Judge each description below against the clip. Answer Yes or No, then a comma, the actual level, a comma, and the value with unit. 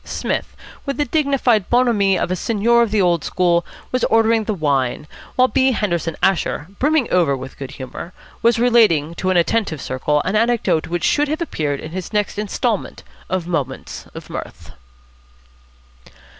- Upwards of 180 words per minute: No, average, 165 wpm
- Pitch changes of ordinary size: No, wide, 6.2 semitones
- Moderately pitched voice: No, high, 195 Hz